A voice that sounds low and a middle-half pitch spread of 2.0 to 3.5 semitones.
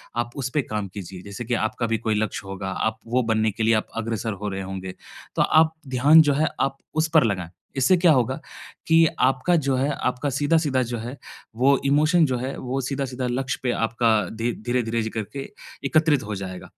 No: low, 125 Hz; average, 4.1 semitones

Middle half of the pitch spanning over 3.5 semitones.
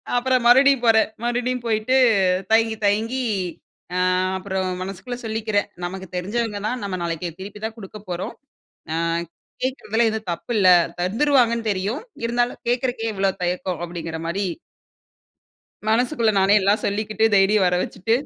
Yes: average, 3.9 semitones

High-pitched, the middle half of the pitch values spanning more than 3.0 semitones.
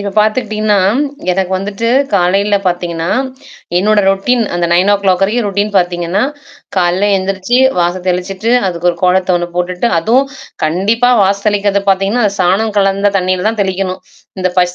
No: high, 195 Hz; narrow, 2.4 semitones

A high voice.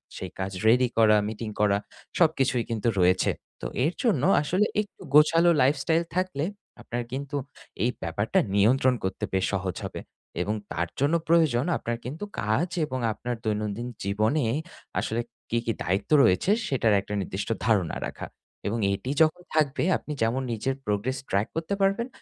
No: low, 120 Hz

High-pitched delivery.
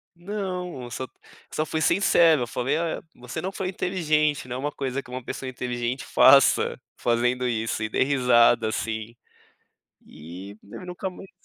No: low, 130 Hz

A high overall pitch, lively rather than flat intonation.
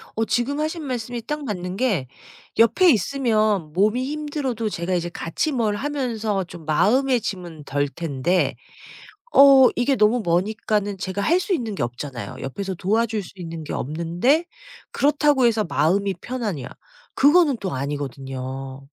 Yes: high, 210 Hz; wide, 7.3 semitones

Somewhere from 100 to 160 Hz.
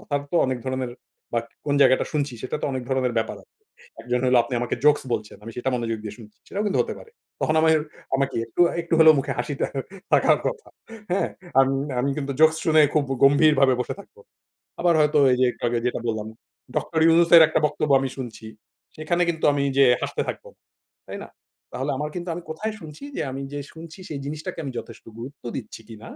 Yes: medium, 140 Hz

